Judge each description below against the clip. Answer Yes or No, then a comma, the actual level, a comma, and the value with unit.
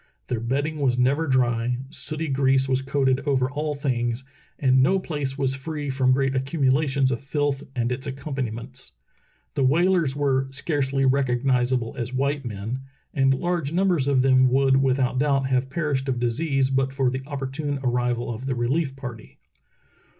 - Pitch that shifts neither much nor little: No, narrow, 1.7 semitones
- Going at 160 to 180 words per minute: Yes, average, 165 wpm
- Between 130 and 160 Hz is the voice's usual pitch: Yes, low, 135 Hz